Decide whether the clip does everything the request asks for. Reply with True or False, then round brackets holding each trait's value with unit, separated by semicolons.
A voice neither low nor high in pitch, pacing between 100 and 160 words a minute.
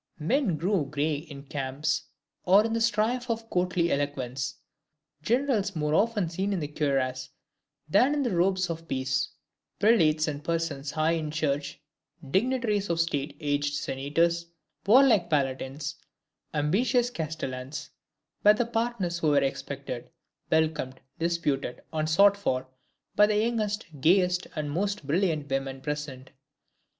True (160 Hz; 135 wpm)